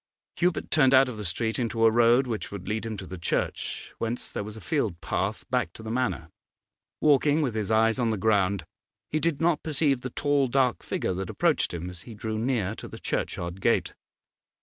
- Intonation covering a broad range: No, average, 4.5 semitones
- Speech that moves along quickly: Yes, fast, 215 wpm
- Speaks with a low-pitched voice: Yes, low, 115 Hz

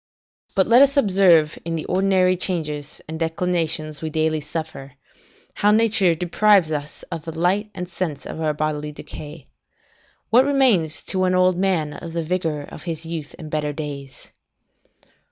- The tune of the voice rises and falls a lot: No, average, 3.2 semitones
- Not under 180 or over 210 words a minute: No, average, 160 wpm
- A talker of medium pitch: Yes, medium, 165 Hz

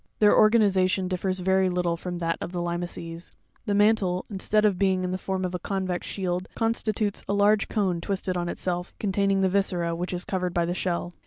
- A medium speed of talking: No, fast, 215 wpm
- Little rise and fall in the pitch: Yes, narrow, 2.1 semitones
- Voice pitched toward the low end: No, medium, 185 Hz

